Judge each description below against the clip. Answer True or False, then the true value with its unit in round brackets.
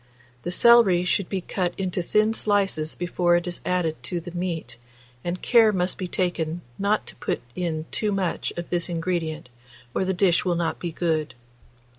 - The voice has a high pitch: False (180 Hz)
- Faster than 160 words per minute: True (180 wpm)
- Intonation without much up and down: True (2.0 semitones)